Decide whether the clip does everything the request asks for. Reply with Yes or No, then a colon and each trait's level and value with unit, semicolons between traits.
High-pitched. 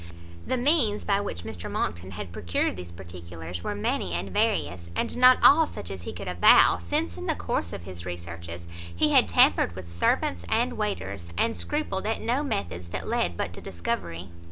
No: very low, 90 Hz